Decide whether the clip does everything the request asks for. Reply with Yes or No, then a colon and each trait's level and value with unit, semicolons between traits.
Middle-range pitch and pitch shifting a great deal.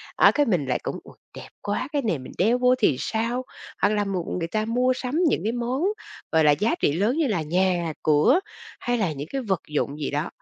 No: high, 205 Hz; wide, 7.4 semitones